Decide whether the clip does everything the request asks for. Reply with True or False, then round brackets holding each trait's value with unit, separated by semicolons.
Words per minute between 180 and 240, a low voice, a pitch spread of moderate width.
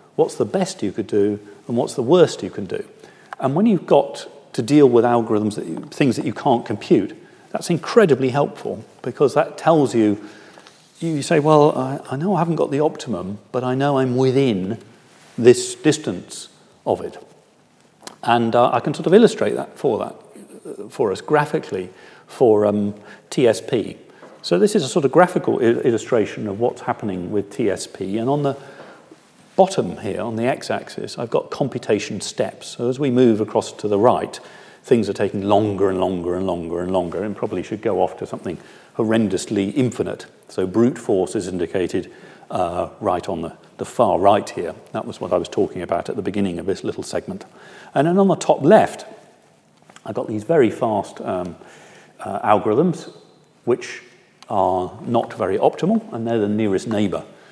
False (185 wpm; 120 Hz; 5.7 semitones)